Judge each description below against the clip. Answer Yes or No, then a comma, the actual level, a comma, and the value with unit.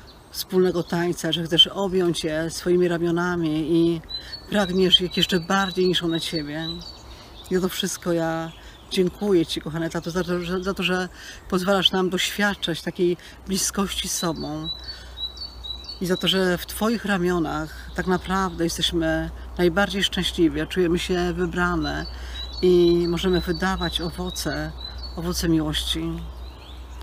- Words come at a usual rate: Yes, average, 130 wpm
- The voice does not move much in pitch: Yes, narrow, 2.2 semitones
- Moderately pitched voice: Yes, medium, 175 Hz